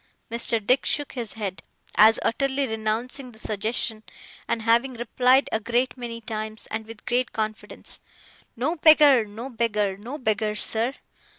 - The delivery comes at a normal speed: Yes, average, 150 wpm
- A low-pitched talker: No, high, 230 Hz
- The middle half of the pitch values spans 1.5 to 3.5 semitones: Yes, average, 2.7 semitones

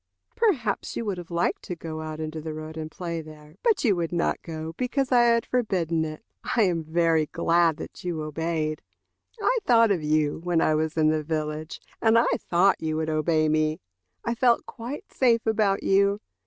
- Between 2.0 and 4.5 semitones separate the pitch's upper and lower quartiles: No, average, 5.2 semitones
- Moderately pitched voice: Yes, medium, 165 Hz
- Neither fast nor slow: Yes, average, 195 wpm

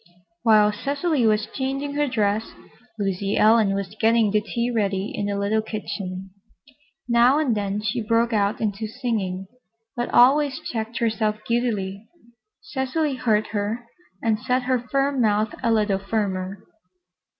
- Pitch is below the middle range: No, high, 220 Hz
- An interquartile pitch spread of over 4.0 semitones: No, average, 3.1 semitones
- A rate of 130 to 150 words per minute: Yes, average, 140 wpm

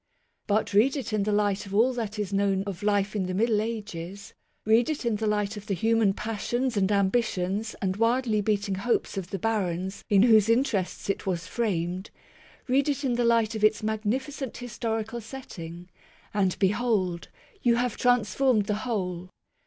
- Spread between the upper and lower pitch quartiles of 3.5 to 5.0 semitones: No, average, 3.0 semitones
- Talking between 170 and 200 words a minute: Yes, average, 180 wpm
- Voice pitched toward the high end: Yes, high, 210 Hz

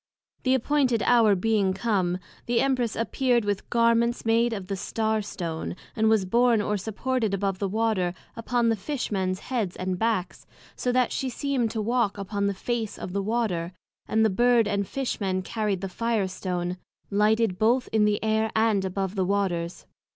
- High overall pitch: Yes, high, 215 Hz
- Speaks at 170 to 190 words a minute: Yes, average, 180 wpm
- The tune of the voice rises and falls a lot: No, average, 3.3 semitones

